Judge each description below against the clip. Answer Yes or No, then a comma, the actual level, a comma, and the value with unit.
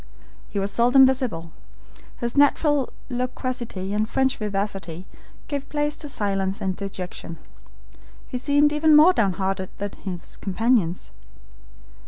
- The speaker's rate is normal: No, slow, 120 wpm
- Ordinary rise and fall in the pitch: No, wide, 5.7 semitones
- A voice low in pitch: No, high, 225 Hz